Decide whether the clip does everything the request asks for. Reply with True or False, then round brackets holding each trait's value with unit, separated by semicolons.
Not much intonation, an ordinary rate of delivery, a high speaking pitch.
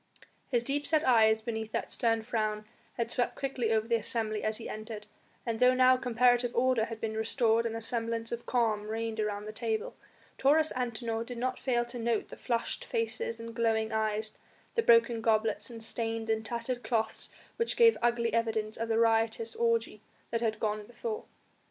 True (1.6 semitones; 185 wpm; 230 Hz)